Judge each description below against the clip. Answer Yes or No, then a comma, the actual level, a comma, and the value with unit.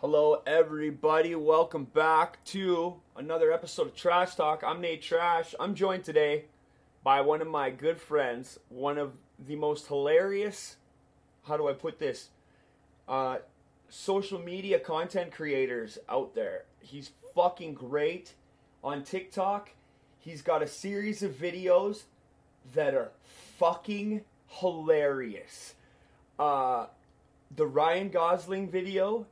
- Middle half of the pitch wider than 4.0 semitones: Yes, average, 4.4 semitones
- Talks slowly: Yes, slow, 120 wpm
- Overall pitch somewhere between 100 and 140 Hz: No, medium, 160 Hz